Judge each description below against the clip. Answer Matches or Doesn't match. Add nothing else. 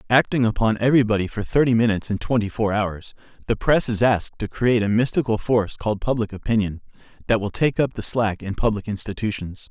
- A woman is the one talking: Doesn't match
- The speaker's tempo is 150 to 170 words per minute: Doesn't match